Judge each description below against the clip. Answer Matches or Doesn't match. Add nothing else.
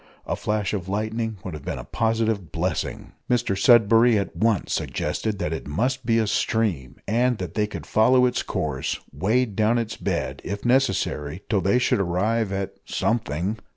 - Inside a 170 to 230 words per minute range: Matches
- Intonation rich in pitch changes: Doesn't match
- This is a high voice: Doesn't match